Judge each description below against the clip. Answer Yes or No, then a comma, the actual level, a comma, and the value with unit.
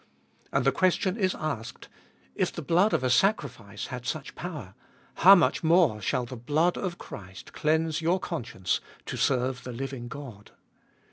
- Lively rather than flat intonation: Yes, wide, 6.2 semitones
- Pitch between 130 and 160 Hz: Yes, medium, 140 Hz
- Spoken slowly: No, average, 165 wpm